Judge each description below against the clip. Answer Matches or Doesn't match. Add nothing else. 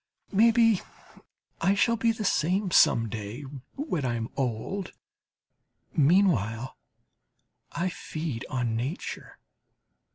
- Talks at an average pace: Doesn't match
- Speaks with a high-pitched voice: Doesn't match